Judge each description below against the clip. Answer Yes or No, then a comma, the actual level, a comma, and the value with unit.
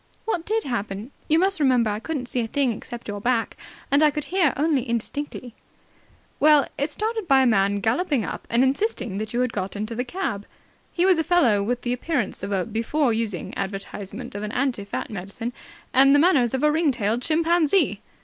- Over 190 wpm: Yes, fast, 205 wpm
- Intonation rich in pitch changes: Yes, wide, 5.8 semitones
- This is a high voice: Yes, very high, 250 Hz